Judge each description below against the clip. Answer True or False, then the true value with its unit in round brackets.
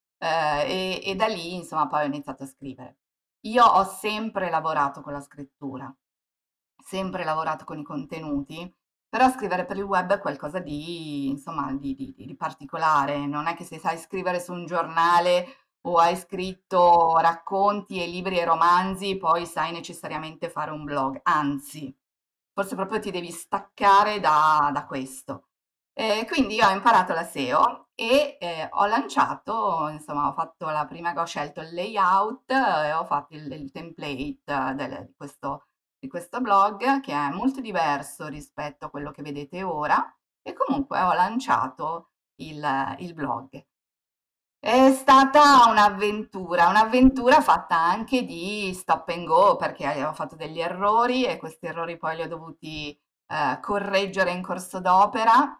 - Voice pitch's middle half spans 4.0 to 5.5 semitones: True (4.9 semitones)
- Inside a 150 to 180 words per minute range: True (155 wpm)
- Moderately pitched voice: True (170 Hz)